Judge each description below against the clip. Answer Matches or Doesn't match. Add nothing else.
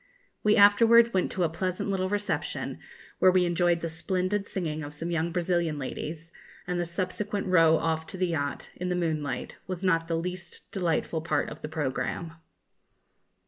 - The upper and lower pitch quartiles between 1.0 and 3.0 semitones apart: Matches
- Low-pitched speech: Doesn't match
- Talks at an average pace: Matches